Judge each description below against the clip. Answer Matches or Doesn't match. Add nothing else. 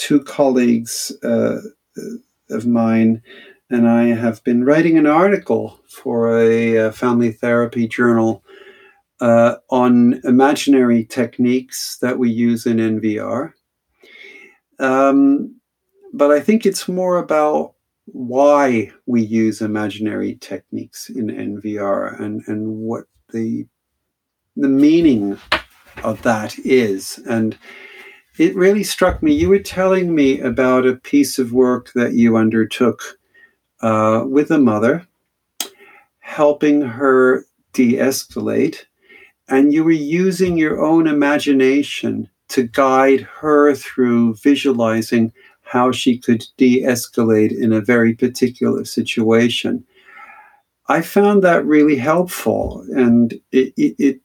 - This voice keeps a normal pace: Doesn't match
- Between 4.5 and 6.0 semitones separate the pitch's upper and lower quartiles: Matches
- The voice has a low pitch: Matches